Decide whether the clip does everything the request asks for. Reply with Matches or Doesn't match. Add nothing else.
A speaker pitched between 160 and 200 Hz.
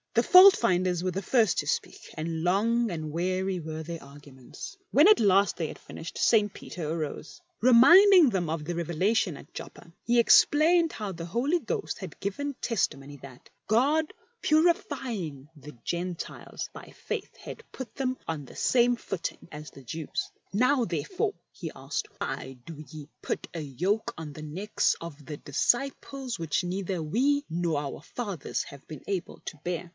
Matches